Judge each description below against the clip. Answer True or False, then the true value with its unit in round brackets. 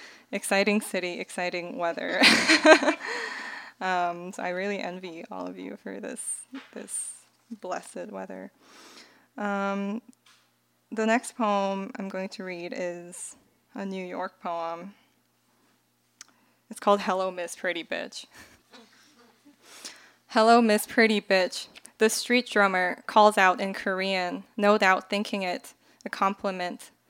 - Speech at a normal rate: False (115 wpm)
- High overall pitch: True (200 Hz)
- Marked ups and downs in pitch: False (3.9 semitones)